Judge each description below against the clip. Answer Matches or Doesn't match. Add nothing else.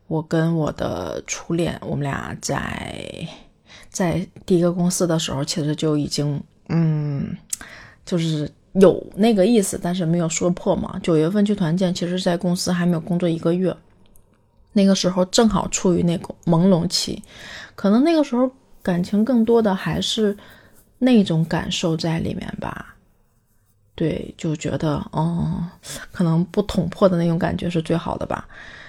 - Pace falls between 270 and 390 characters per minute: Doesn't match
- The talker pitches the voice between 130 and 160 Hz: Doesn't match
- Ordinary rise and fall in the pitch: Matches